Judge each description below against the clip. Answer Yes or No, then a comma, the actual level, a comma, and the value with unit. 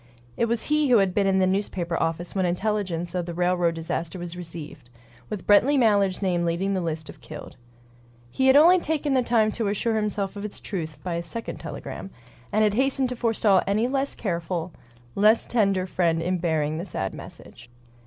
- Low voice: No, high, 190 Hz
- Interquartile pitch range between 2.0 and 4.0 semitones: No, average, 4.5 semitones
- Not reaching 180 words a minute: No, average, 195 wpm